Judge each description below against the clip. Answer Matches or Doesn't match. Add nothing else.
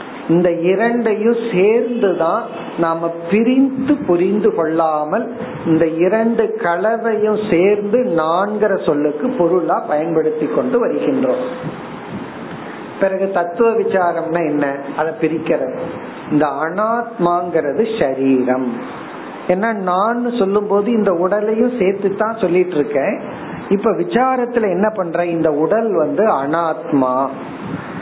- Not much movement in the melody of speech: Doesn't match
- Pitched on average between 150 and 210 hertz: Matches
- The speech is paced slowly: Doesn't match